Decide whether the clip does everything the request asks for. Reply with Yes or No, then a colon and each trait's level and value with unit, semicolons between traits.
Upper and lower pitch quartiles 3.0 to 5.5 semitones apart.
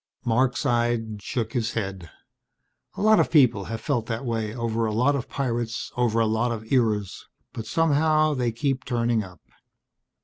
No: narrow, 2.4 semitones